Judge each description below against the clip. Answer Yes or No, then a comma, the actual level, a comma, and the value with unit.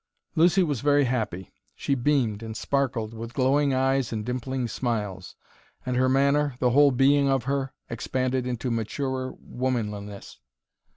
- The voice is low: Yes, low, 130 Hz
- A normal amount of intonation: Yes, average, 3.1 semitones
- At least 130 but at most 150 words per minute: Yes, average, 140 wpm